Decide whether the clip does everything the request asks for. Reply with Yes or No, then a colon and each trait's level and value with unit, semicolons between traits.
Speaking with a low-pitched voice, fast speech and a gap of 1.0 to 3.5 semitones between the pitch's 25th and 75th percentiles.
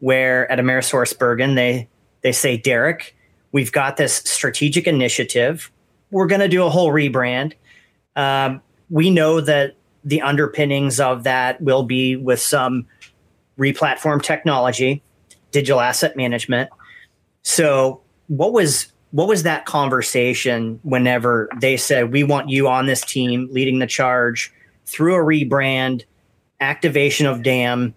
No: low, 130 Hz; slow, 135 wpm; narrow, 2.5 semitones